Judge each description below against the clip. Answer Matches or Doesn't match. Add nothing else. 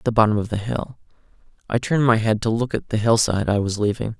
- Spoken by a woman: Doesn't match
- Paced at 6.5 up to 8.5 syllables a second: Matches